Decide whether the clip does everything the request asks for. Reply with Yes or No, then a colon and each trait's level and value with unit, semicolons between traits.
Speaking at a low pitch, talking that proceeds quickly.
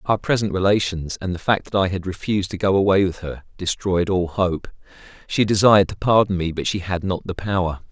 Yes: very low, 95 Hz; fast, 220 wpm